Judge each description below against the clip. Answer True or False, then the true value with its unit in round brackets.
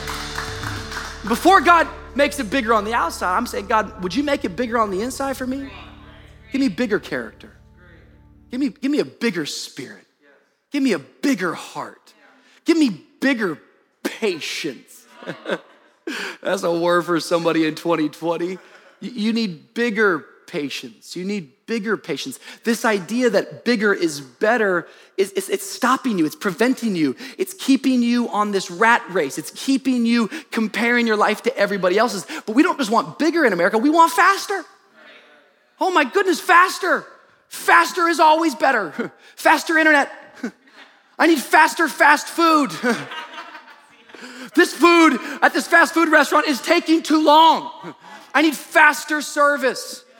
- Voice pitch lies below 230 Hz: False (260 Hz)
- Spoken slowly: False (150 wpm)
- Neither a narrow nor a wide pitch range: False (7.0 semitones)